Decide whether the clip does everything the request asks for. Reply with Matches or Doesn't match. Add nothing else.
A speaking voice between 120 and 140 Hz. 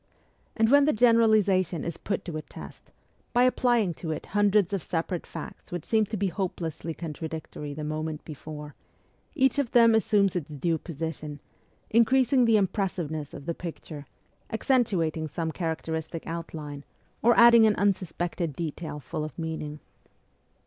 Doesn't match